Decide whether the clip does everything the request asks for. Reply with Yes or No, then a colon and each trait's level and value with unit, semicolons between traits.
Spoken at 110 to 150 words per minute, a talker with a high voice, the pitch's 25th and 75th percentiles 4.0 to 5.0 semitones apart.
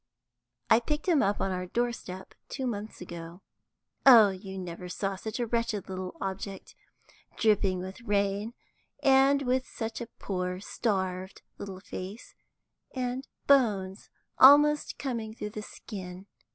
Yes: average, 140 wpm; high, 205 Hz; average, 4.3 semitones